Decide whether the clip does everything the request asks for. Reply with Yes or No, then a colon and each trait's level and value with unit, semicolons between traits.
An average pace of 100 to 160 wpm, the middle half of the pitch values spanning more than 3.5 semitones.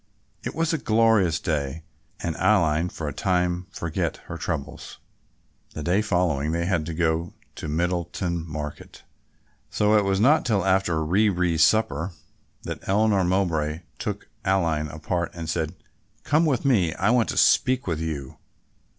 Yes: average, 155 wpm; average, 4.2 semitones